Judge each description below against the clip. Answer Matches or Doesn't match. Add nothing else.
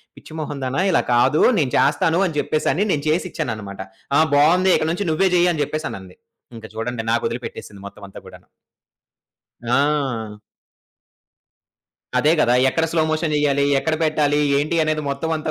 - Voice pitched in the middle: Matches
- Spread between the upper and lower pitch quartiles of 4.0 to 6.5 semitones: Matches